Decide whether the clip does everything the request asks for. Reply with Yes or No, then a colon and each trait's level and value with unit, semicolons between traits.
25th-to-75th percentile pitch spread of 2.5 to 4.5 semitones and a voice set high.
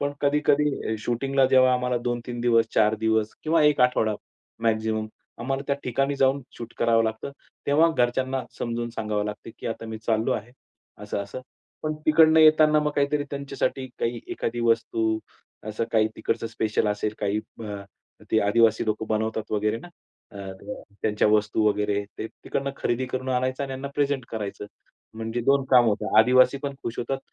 No: average, 3.7 semitones; low, 120 Hz